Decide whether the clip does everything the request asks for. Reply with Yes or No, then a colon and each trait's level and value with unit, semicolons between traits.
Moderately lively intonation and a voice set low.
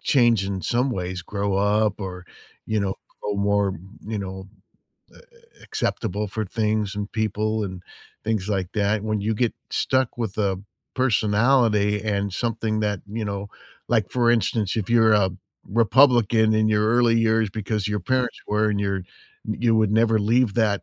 No: narrow, 2.1 semitones; low, 105 Hz